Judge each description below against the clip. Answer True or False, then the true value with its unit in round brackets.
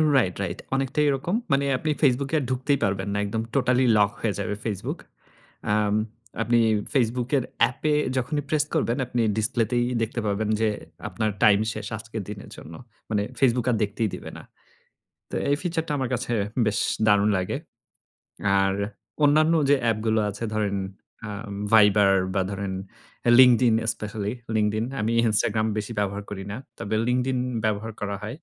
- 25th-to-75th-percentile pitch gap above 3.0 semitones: True (3.6 semitones)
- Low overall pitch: True (110 Hz)